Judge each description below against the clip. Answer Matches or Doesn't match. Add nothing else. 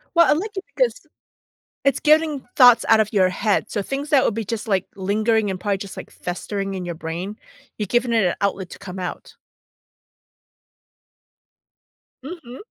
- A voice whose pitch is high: Matches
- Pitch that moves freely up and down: Matches